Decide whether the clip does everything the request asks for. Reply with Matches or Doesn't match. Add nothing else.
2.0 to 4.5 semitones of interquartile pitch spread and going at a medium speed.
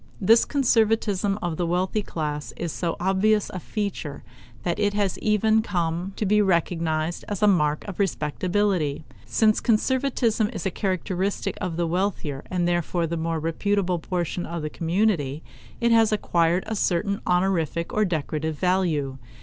Matches